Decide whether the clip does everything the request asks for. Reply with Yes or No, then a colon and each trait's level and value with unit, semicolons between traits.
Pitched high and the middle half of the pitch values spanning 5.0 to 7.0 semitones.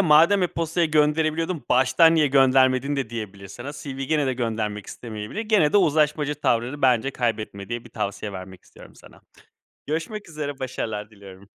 No: low, 135 Hz; wide, 5.6 semitones